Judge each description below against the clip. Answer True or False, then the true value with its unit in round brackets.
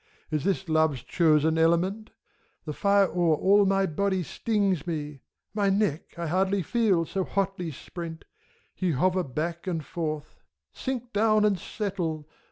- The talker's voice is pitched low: False (180 Hz)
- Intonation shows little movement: False (3.8 semitones)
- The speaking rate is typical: True (150 wpm)